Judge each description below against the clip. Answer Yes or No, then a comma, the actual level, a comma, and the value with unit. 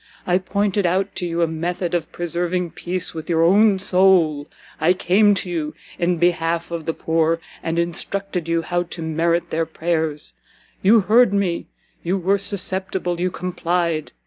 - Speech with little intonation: Yes, narrow, 2.1 semitones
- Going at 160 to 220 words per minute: Yes, average, 165 wpm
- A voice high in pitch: No, medium, 175 Hz